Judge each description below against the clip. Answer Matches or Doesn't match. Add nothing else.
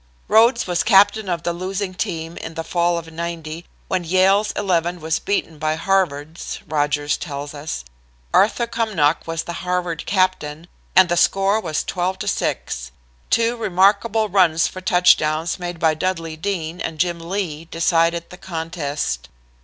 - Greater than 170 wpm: Doesn't match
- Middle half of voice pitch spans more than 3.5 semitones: Doesn't match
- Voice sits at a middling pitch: Matches